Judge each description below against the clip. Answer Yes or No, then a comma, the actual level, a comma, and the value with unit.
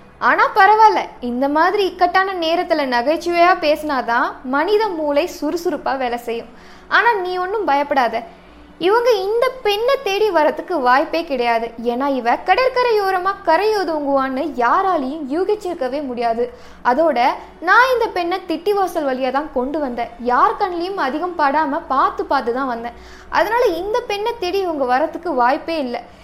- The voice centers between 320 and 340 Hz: Yes, very high, 325 Hz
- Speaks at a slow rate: No, fast, 130 wpm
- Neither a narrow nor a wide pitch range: No, wide, 6.4 semitones